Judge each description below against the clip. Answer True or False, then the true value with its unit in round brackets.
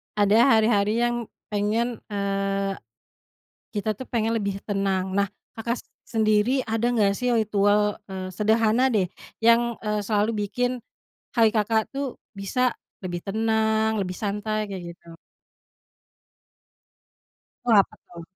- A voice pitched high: True (215 Hz)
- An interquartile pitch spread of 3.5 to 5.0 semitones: False (2.4 semitones)